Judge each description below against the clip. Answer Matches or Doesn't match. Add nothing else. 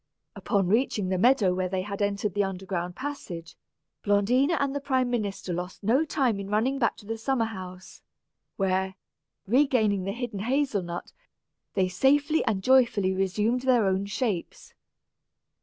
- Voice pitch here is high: Matches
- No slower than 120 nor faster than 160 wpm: Matches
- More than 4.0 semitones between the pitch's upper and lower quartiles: Matches